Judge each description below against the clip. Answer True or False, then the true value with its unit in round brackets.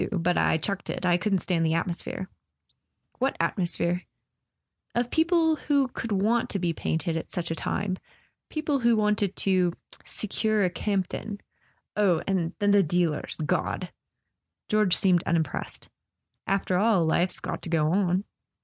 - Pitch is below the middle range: False (190 Hz)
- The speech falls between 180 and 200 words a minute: False (160 wpm)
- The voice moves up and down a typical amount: True (3.6 semitones)